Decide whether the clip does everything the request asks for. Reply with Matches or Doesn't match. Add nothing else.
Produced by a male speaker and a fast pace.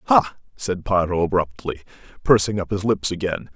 Doesn't match